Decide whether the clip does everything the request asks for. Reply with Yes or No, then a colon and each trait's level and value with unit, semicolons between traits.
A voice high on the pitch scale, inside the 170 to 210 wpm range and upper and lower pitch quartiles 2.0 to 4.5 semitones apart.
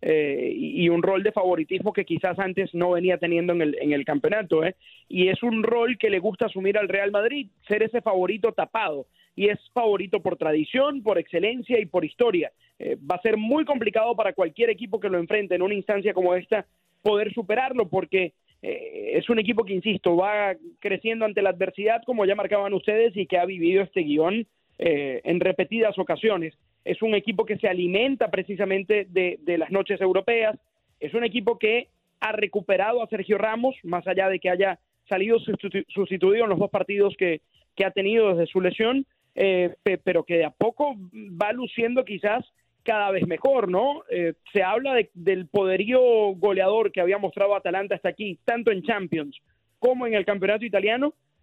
Yes: high, 200 Hz; fast, 190 wpm; average, 3.4 semitones